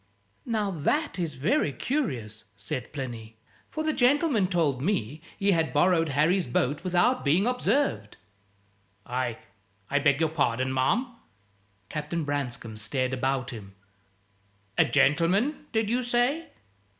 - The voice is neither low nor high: Yes, medium, 155 Hz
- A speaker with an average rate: No, slow, 125 wpm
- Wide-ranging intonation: Yes, wide, 8.9 semitones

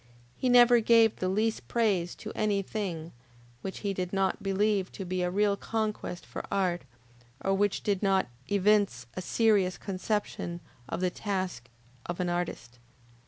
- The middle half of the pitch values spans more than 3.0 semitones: No, narrow, 2.6 semitones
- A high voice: Yes, high, 195 Hz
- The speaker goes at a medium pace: Yes, average, 160 wpm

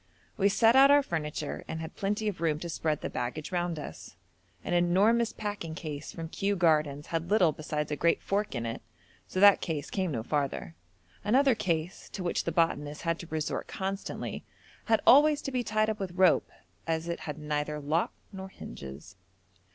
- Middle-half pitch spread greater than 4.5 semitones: Yes, average, 5.0 semitones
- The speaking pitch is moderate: Yes, medium, 170 Hz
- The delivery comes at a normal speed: Yes, average, 190 wpm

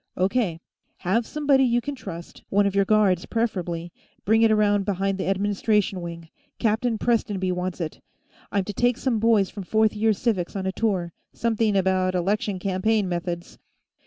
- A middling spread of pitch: Yes, average, 3.2 semitones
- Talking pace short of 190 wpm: Yes, average, 170 wpm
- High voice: Yes, high, 200 Hz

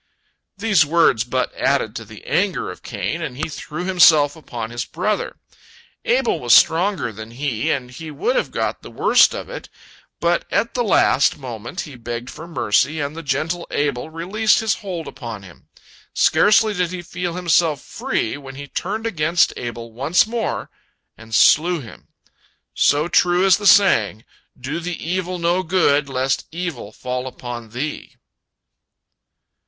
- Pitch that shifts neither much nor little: No, wide, 6.0 semitones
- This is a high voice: No, medium, 155 Hz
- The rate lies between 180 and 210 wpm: No, average, 160 wpm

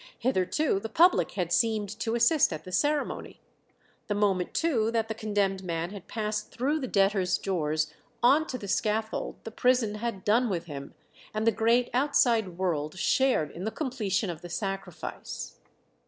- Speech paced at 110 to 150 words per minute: No, average, 170 wpm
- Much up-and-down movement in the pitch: No, average, 4.2 semitones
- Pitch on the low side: No, high, 215 Hz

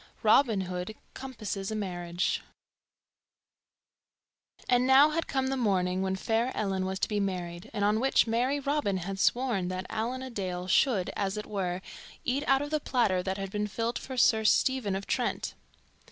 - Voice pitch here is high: Yes, high, 210 Hz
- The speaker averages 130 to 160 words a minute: No, average, 175 wpm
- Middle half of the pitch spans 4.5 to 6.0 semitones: Yes, average, 5.1 semitones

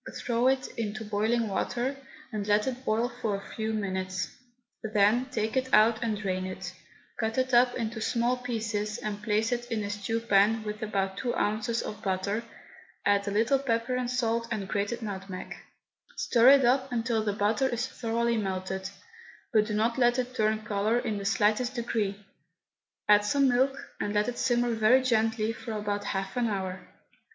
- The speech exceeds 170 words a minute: Yes, average, 180 wpm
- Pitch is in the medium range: No, high, 220 Hz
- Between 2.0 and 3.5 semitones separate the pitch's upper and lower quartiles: Yes, average, 2.8 semitones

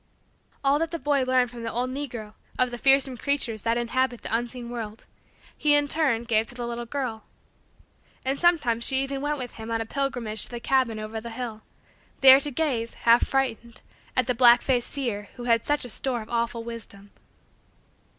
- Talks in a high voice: Yes, high, 245 Hz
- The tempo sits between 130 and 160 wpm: No, average, 195 wpm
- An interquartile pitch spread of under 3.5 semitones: Yes, average, 2.8 semitones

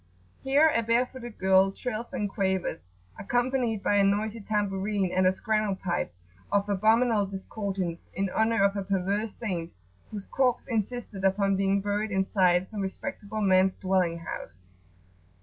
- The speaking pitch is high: Yes, high, 200 Hz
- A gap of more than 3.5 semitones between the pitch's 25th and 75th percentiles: No, narrow, 2.5 semitones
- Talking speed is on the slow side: No, average, 150 wpm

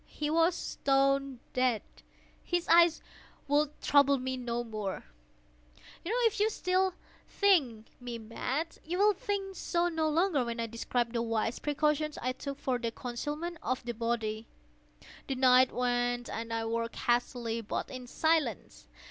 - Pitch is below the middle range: No, very high, 260 Hz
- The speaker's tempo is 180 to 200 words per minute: No, average, 150 wpm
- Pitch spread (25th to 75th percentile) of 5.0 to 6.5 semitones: Yes, average, 5.3 semitones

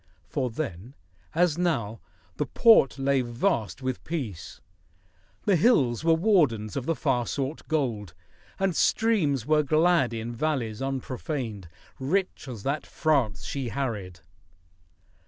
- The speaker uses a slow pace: Yes, slow, 125 wpm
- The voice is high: No, low, 135 Hz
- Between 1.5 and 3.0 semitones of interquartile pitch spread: No, wide, 5.4 semitones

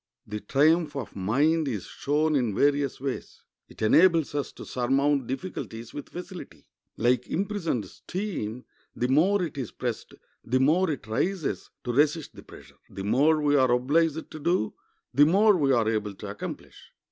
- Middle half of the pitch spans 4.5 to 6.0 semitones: Yes, average, 4.9 semitones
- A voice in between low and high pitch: Yes, medium, 145 Hz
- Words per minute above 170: No, average, 165 wpm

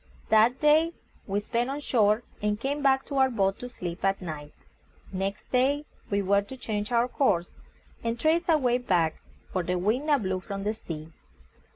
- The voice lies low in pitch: No, high, 220 Hz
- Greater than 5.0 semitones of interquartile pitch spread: Yes, wide, 5.4 semitones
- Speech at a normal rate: Yes, average, 190 wpm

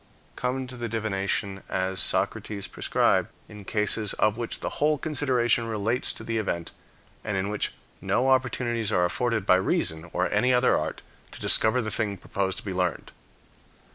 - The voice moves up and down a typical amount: Yes, average, 3.9 semitones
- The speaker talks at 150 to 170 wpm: Yes, average, 165 wpm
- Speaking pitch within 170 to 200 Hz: No, low, 110 Hz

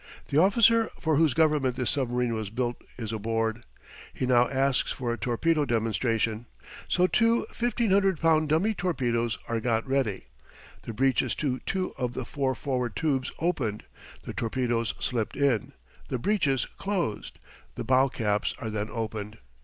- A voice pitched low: Yes, low, 130 Hz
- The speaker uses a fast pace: No, average, 155 wpm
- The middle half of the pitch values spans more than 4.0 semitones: Yes, wide, 5.4 semitones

